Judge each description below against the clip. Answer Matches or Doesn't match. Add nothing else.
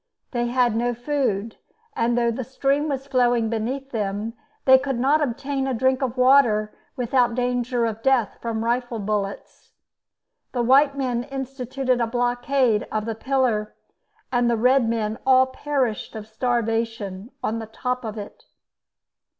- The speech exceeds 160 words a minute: Doesn't match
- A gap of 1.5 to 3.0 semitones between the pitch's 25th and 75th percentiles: Matches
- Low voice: Doesn't match